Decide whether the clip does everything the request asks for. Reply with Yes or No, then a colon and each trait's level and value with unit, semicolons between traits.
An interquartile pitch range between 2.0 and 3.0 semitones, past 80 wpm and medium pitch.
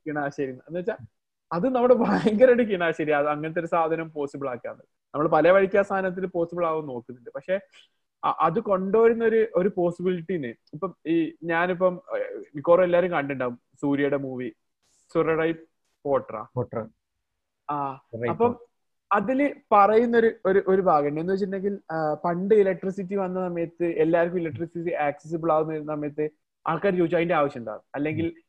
No: average, 4.7 semitones; average, 120 wpm; medium, 170 Hz